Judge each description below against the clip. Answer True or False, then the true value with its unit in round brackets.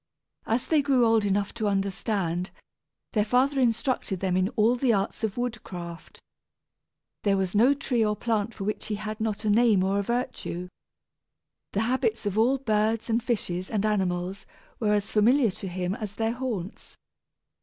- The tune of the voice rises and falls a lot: False (3.3 semitones)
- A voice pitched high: True (215 Hz)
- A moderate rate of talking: True (170 wpm)